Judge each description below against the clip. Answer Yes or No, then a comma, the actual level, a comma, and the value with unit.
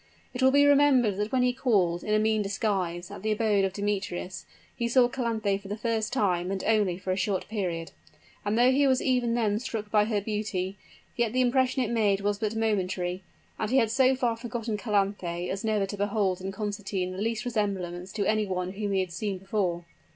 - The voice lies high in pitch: Yes, high, 210 Hz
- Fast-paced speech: Yes, fast, 215 wpm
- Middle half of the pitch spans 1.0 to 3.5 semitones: Yes, average, 3.2 semitones